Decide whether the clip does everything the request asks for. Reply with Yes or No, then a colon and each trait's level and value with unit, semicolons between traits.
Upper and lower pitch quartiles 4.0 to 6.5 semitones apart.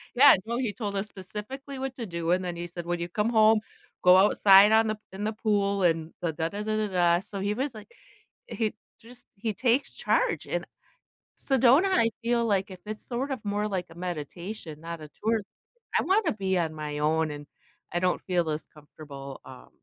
Yes: average, 4.7 semitones